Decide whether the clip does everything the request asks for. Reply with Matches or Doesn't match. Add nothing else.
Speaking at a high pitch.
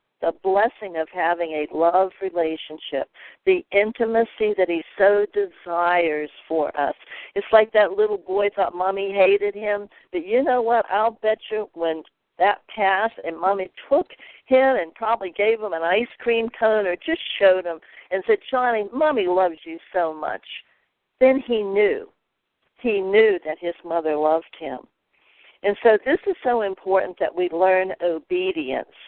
Matches